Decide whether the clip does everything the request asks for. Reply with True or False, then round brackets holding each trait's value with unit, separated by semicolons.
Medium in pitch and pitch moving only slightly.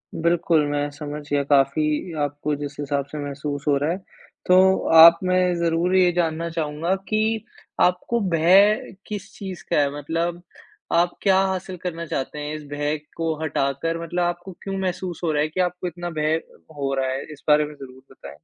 False (165 Hz; 3.5 semitones)